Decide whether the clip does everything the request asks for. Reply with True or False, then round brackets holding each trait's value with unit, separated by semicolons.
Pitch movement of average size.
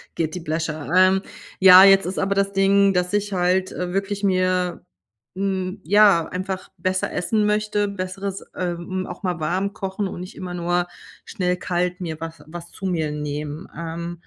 False (2.1 semitones)